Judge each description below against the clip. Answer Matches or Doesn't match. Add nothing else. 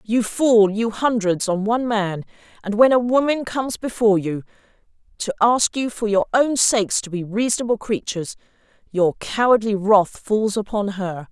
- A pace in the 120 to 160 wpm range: Matches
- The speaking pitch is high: Matches